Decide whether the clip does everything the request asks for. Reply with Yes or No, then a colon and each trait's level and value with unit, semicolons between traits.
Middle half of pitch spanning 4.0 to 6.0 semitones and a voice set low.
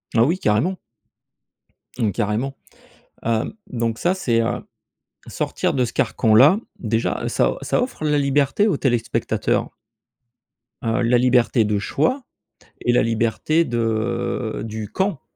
Yes: average, 4.4 semitones; low, 120 Hz